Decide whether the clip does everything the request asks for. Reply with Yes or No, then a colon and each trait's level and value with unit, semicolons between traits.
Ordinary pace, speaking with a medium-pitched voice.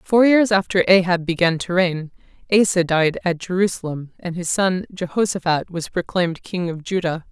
Yes: average, 165 wpm; medium, 180 Hz